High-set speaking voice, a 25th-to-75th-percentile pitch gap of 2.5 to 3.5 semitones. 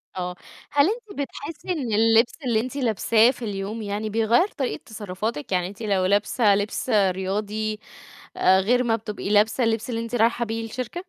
Yes: high, 220 Hz; average, 2.9 semitones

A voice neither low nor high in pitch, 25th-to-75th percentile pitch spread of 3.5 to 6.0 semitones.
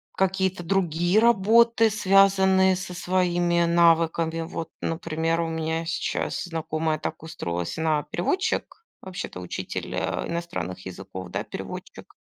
No: medium, 170 Hz; average, 2.8 semitones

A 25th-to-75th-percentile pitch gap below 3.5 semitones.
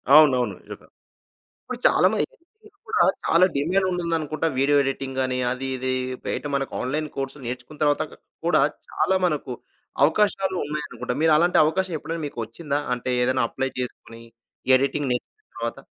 No: average, 4.5 semitones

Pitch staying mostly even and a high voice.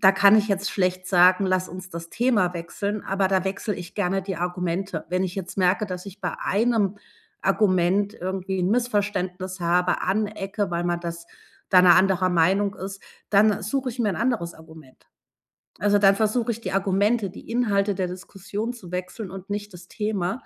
Yes: narrow, 2.3 semitones; high, 195 Hz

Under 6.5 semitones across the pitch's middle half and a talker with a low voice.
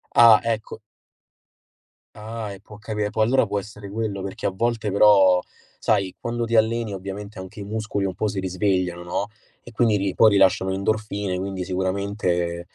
Yes: narrow, 2.5 semitones; low, 100 Hz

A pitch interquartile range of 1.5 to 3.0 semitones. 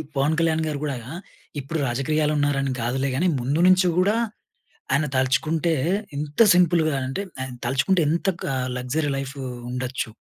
No: average, 3.4 semitones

